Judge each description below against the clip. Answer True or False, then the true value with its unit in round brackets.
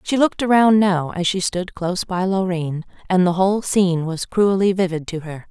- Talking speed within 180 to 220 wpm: True (205 wpm)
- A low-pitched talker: False (185 Hz)